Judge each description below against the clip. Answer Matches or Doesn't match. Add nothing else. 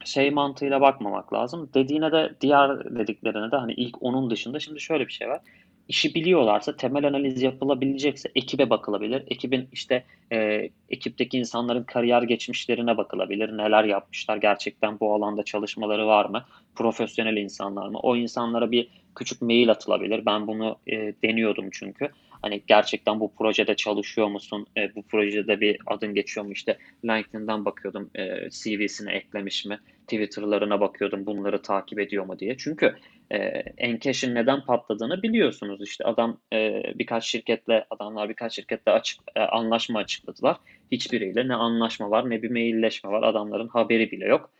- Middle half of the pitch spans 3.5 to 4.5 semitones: Doesn't match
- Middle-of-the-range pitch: Doesn't match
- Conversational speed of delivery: Doesn't match